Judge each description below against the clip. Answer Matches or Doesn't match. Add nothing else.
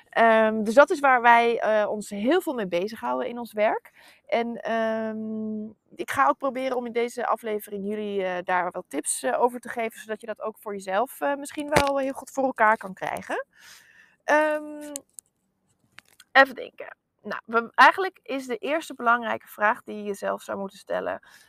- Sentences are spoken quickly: Doesn't match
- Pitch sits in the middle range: Doesn't match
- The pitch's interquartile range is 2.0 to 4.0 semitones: Doesn't match